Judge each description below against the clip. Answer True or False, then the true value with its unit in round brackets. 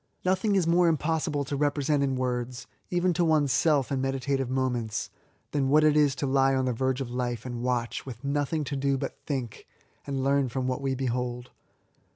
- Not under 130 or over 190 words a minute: False (200 wpm)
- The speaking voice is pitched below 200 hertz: True (135 Hz)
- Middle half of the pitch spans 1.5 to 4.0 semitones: True (2.5 semitones)